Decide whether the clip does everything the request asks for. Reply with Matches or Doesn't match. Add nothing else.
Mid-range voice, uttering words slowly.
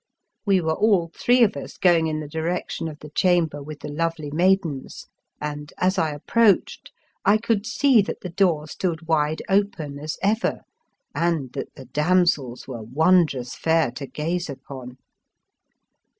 Doesn't match